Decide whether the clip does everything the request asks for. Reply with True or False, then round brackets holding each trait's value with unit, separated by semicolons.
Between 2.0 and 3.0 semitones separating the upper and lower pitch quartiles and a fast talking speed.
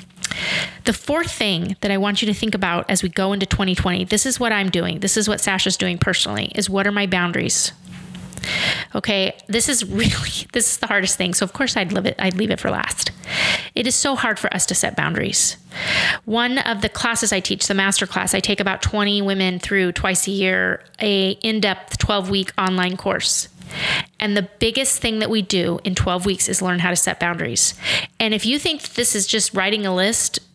True (2.6 semitones; 215 wpm)